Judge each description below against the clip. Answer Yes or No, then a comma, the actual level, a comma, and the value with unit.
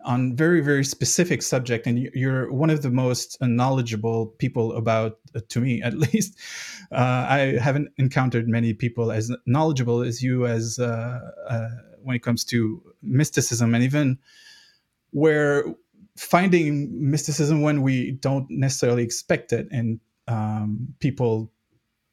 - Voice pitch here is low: Yes, low, 125 Hz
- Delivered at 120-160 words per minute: Yes, slow, 135 wpm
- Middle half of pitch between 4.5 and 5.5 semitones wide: No, average, 3.7 semitones